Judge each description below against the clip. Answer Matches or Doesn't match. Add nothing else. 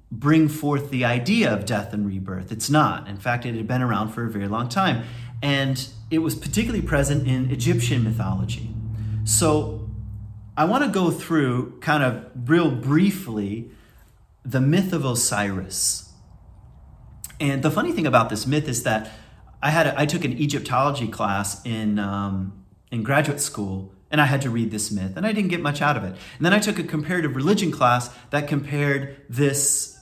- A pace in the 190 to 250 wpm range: Doesn't match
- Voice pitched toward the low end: Matches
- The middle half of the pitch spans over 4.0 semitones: Matches